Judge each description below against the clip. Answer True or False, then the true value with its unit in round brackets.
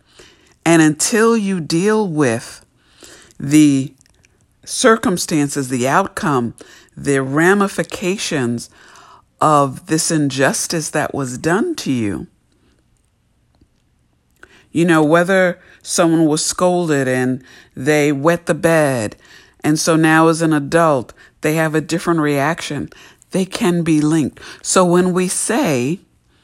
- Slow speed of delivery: True (110 wpm)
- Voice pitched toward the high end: False (160 Hz)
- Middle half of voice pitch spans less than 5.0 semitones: True (3.8 semitones)